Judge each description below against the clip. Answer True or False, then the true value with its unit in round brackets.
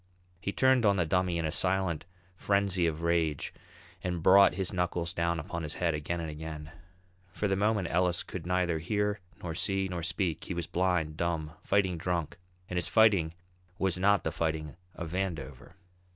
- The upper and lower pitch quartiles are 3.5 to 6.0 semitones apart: False (2.7 semitones)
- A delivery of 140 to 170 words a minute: False (180 wpm)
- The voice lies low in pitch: True (90 Hz)